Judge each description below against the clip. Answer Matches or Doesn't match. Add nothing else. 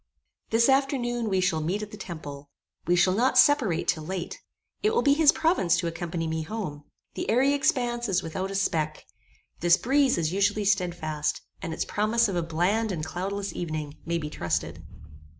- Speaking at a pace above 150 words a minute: Matches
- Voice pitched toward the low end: Doesn't match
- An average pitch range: Doesn't match